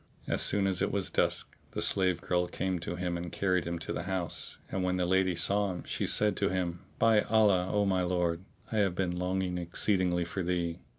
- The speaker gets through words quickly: Yes, fast, 220 wpm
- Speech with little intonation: Yes, narrow, 1.6 semitones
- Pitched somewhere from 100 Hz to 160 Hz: No, very low, 90 Hz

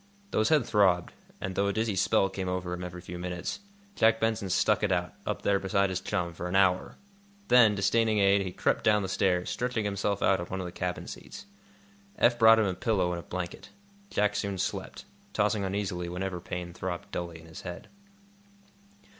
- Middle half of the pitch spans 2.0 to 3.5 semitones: Yes, average, 2.8 semitones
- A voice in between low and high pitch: No, very low, 95 Hz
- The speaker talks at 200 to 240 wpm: Yes, fast, 205 wpm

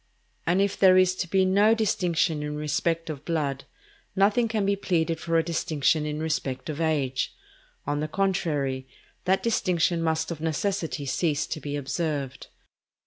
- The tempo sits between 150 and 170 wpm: Yes, average, 160 wpm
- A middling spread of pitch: Yes, average, 3.8 semitones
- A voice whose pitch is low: No, medium, 165 Hz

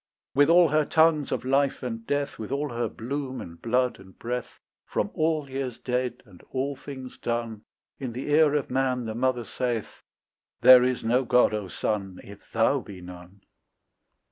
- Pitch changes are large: No, average, 3.6 semitones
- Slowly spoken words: No, average, 175 wpm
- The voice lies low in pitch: Yes, low, 125 Hz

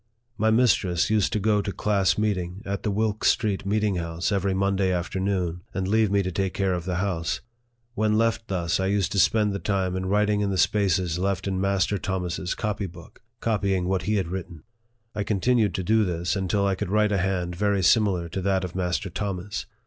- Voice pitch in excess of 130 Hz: No, very low, 95 Hz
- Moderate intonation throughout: No, narrow, 2.2 semitones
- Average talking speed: No, fast, 210 wpm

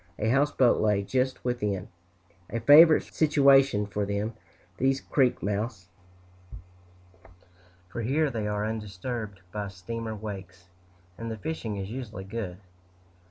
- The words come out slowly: Yes, slow, 120 wpm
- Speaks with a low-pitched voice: Yes, low, 110 Hz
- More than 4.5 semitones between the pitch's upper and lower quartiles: No, average, 4.1 semitones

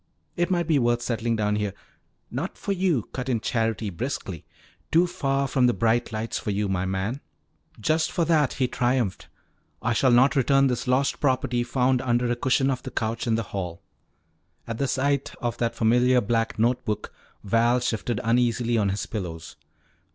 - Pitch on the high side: No, low, 120 Hz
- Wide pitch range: No, average, 3.0 semitones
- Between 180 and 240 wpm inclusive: Yes, average, 185 wpm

